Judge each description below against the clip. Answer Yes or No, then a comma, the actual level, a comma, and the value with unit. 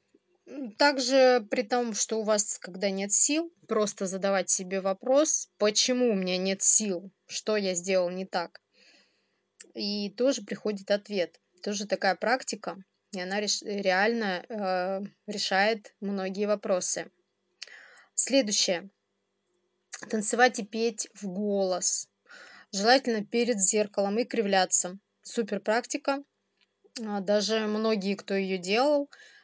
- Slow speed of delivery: Yes, slow, 110 wpm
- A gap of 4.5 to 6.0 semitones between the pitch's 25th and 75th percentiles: No, average, 3.6 semitones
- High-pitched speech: Yes, high, 210 Hz